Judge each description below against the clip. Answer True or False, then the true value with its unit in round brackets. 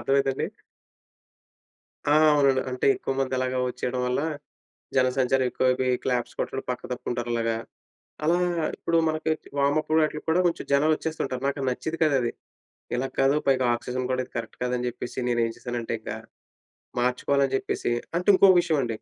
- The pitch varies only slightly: True (2.2 semitones)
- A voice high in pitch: False (130 Hz)